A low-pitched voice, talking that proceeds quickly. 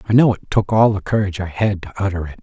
Yes: low, 100 Hz; fast, 295 wpm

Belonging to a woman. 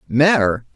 No: male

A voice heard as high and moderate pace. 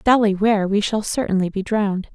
Yes: high, 205 Hz; average, 195 wpm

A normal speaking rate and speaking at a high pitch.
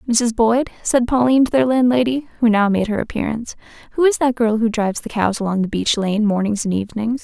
No: fast, 225 wpm; high, 225 Hz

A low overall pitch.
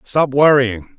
Yes: low, 130 Hz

